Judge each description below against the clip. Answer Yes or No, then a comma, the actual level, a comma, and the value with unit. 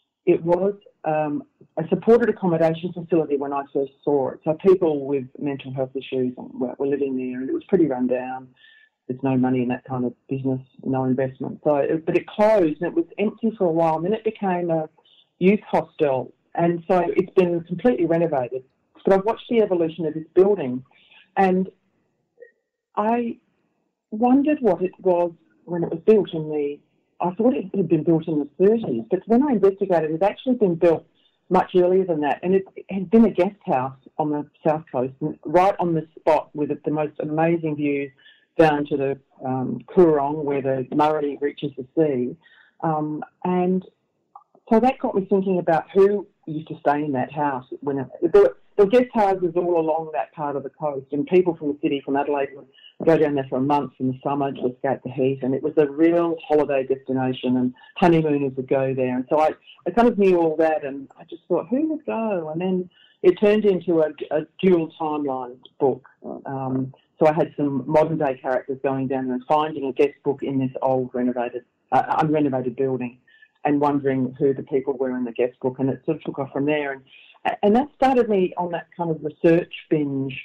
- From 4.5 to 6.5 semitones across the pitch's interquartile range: Yes, average, 5.2 semitones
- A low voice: No, medium, 155 Hz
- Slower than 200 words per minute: No, fast, 205 wpm